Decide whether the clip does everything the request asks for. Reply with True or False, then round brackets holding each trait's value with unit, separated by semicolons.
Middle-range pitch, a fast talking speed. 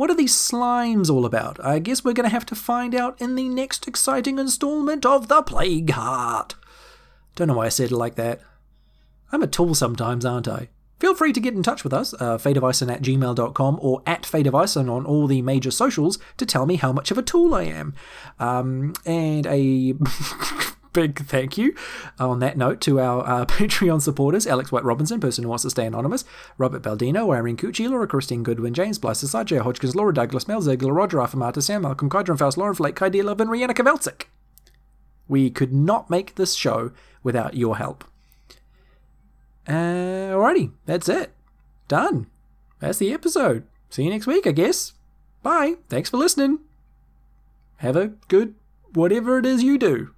False (160 Hz; 180 wpm)